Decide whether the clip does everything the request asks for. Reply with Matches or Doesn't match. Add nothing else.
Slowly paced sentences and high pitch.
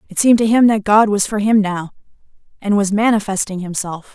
Doesn't match